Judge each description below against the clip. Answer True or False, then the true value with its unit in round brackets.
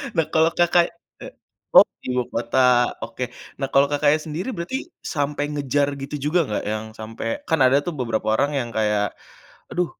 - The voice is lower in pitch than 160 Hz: True (140 Hz)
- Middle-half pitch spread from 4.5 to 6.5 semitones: True (5.1 semitones)